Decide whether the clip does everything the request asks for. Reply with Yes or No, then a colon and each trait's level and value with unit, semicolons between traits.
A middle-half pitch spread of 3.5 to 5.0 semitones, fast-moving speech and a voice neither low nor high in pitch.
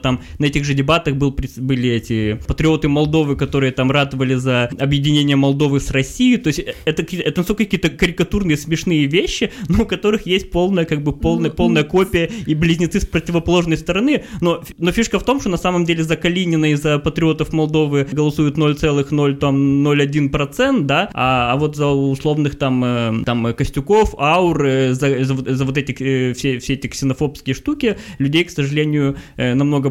Yes: average, 3.9 semitones; fast, 170 wpm; medium, 150 Hz